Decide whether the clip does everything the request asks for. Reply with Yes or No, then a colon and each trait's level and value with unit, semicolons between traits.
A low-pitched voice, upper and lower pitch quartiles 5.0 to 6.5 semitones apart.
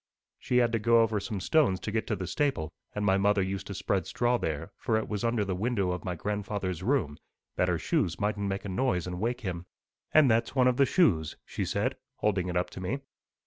No: low, 105 Hz; average, 4.2 semitones